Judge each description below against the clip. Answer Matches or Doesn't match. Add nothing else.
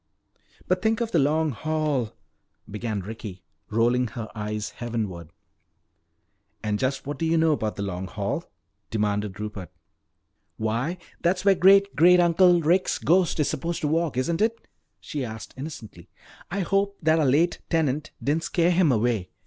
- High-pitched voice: Doesn't match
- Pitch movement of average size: Doesn't match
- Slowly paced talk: Doesn't match